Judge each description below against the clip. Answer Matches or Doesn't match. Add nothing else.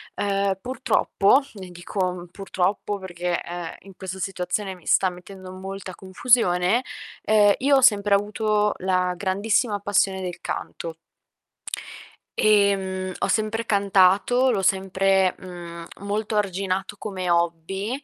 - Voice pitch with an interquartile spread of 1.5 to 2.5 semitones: Matches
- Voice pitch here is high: Matches